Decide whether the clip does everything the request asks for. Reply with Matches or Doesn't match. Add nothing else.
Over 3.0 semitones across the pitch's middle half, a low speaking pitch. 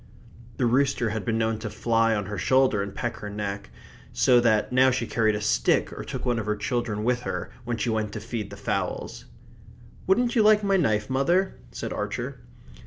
Matches